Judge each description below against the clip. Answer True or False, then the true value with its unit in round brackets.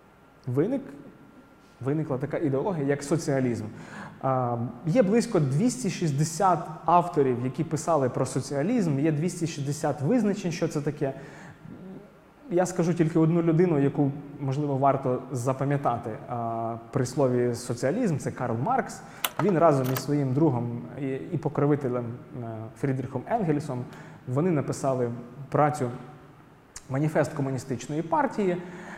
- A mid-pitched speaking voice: True (145 Hz)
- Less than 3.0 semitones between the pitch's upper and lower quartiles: False (4.2 semitones)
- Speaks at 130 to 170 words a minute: False (105 wpm)